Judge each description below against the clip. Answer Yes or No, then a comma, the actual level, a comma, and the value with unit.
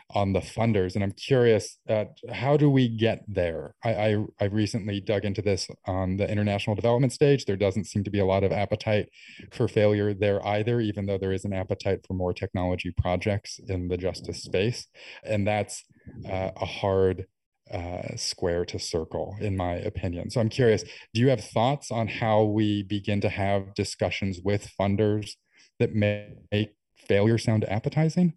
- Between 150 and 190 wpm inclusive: Yes, average, 180 wpm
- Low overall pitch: Yes, low, 105 Hz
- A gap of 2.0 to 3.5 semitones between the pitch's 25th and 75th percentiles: Yes, narrow, 2.4 semitones